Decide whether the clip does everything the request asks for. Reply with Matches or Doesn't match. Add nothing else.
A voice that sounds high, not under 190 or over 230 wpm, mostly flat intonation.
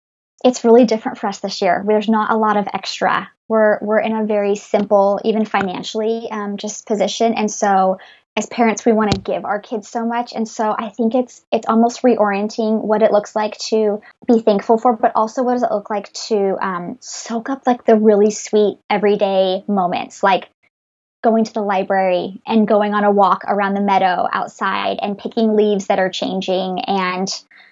Matches